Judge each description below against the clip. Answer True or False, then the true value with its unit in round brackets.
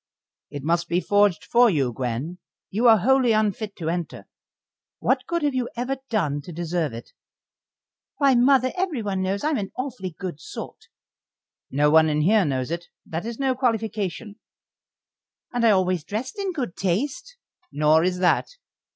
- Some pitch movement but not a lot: False (6.7 semitones)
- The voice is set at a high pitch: True (200 Hz)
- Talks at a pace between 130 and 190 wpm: True (160 wpm)